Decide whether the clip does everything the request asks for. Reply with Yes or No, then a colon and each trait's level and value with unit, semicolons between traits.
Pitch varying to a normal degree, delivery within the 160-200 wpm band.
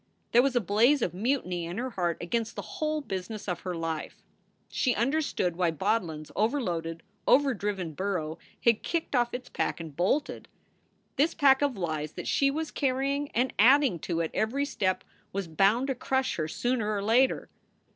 No: wide, 7.1 semitones; average, 180 wpm